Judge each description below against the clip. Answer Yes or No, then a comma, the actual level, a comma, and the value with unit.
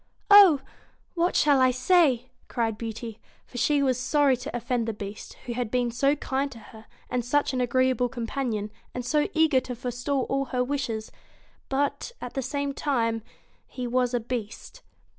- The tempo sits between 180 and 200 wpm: Yes, average, 185 wpm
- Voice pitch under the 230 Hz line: No, very high, 255 Hz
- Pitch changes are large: No, average, 2.8 semitones